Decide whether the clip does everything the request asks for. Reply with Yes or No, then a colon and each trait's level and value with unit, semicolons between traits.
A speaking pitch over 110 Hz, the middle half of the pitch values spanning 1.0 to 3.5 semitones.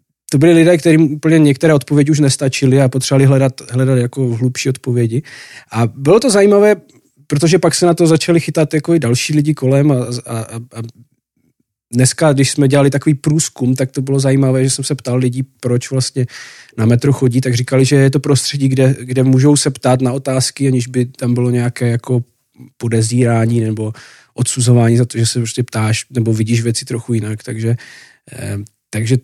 Yes: low, 130 Hz; average, 2.7 semitones